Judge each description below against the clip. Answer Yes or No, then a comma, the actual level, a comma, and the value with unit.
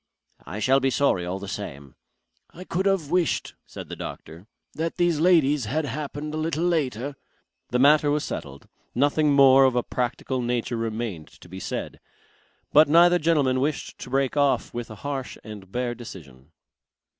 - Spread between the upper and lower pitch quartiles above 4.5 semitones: Yes, average, 5.2 semitones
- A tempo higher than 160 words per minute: Yes, average, 170 wpm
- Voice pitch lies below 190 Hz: Yes, low, 135 Hz